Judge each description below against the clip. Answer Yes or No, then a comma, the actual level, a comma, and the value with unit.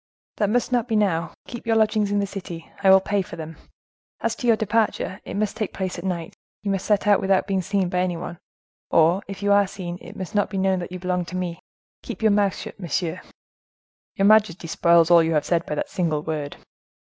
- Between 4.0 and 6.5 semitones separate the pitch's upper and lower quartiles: No, average, 2.9 semitones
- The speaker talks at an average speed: No, fast, 230 wpm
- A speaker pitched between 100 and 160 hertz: No, high, 190 Hz